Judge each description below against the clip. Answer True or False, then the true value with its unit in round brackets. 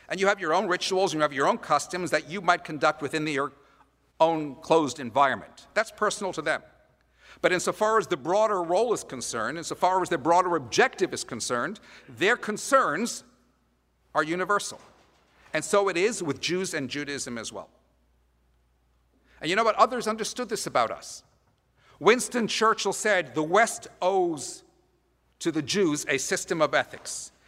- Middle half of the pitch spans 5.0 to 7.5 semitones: True (5.5 semitones)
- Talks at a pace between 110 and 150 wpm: False (170 wpm)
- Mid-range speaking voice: True (180 Hz)